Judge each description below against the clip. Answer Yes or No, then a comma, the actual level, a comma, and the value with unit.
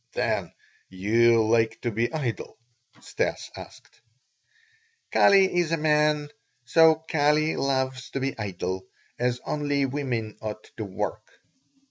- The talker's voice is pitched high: No, low, 130 Hz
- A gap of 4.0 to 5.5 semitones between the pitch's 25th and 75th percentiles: Yes, average, 5.2 semitones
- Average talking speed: No, slow, 120 wpm